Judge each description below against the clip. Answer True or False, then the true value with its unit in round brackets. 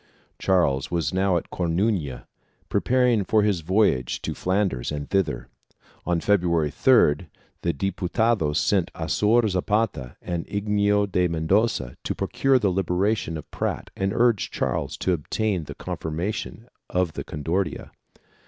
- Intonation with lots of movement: False (4.2 semitones)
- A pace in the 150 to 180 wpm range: False (135 wpm)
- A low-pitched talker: True (95 Hz)